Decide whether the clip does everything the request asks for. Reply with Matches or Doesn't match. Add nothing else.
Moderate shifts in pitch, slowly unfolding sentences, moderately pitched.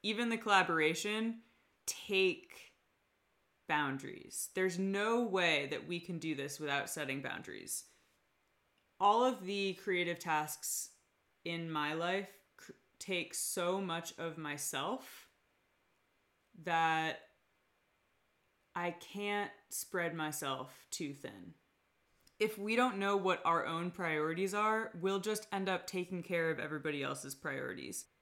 Matches